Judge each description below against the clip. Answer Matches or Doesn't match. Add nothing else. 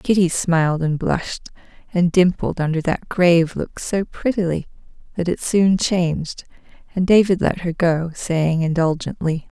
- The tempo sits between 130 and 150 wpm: Matches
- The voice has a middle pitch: Matches